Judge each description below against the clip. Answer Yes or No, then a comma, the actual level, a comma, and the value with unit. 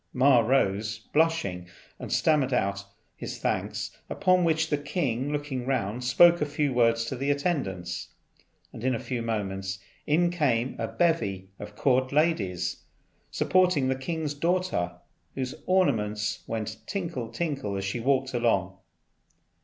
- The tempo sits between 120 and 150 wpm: Yes, average, 140 wpm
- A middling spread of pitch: No, wide, 6.2 semitones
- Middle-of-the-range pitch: No, low, 130 Hz